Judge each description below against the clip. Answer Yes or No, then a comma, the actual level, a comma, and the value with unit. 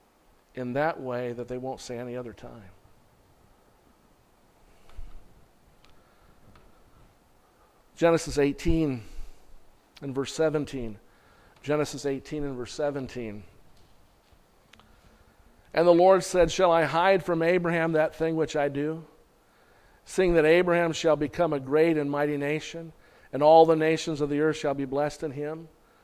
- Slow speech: Yes, slow, 130 wpm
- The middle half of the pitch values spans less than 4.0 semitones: No, average, 4.5 semitones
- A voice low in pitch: No, medium, 145 Hz